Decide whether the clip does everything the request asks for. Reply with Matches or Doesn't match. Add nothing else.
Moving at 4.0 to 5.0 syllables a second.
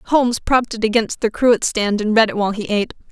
Doesn't match